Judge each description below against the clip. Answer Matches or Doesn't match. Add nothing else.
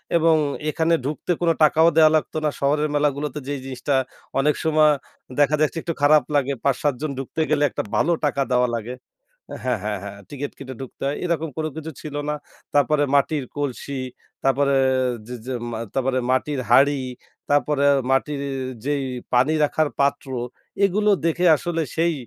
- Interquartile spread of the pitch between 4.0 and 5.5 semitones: Doesn't match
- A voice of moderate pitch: Matches